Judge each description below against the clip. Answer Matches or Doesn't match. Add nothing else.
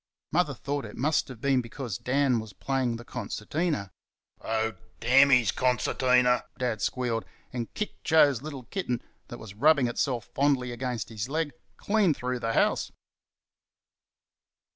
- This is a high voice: Doesn't match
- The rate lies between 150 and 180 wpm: Doesn't match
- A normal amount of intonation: Matches